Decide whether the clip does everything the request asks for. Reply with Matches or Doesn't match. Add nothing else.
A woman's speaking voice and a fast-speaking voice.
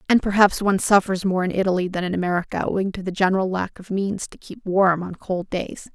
Matches